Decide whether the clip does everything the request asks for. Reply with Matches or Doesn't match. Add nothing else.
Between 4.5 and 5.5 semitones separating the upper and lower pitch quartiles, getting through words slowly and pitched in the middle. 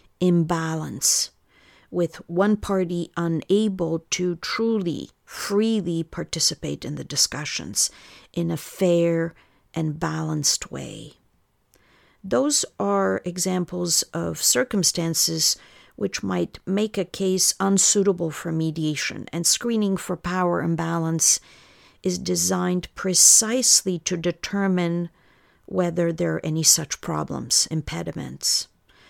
Doesn't match